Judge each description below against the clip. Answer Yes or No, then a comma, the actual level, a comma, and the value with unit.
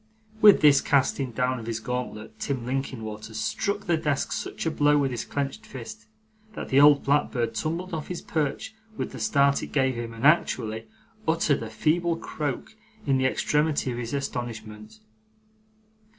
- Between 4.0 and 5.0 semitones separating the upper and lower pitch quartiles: Yes, average, 4.5 semitones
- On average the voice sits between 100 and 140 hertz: Yes, low, 135 Hz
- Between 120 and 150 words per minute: No, average, 165 wpm